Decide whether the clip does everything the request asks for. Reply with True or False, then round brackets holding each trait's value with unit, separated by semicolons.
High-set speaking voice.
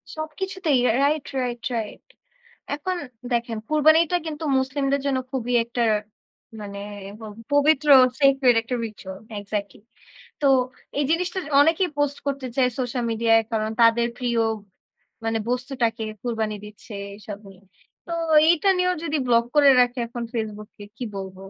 True (250 Hz)